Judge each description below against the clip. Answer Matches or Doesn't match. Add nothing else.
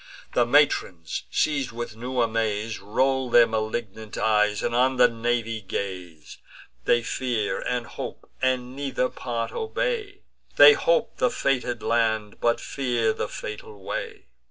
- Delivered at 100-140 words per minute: Matches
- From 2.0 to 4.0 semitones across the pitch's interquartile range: Matches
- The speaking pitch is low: Matches